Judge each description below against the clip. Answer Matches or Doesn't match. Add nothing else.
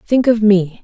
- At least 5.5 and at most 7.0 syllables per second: Doesn't match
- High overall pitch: Matches